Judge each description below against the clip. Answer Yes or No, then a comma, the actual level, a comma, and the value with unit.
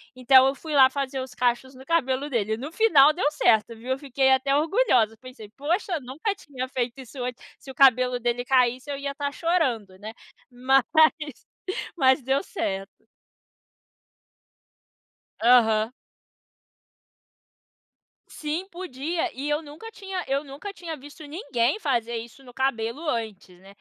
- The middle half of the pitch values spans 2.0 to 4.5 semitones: Yes, average, 3.5 semitones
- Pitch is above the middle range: Yes, very high, 265 Hz